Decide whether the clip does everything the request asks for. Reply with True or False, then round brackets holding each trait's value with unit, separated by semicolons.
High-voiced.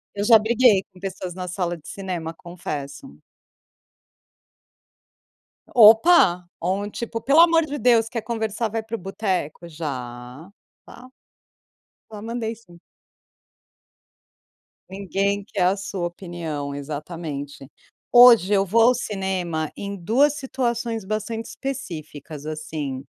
True (195 Hz)